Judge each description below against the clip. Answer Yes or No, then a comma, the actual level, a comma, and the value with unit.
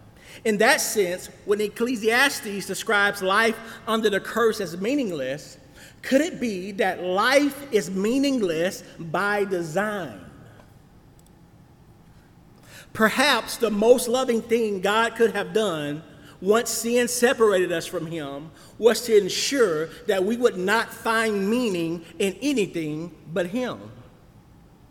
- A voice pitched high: Yes, high, 210 Hz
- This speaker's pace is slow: Yes, slow, 120 wpm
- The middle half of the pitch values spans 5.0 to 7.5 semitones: No, average, 3.9 semitones